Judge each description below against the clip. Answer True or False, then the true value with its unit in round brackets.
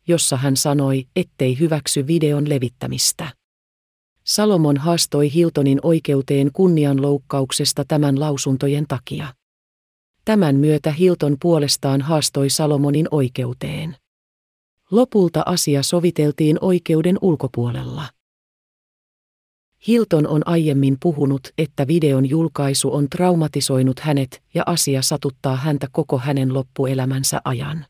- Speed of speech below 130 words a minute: True (95 wpm)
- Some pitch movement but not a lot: True (3.0 semitones)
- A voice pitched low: False (145 Hz)